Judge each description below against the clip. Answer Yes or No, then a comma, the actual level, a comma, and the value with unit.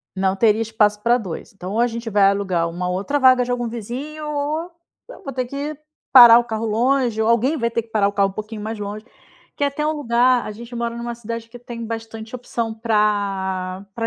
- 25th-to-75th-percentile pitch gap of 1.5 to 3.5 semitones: Yes, average, 2.9 semitones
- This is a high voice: Yes, high, 230 Hz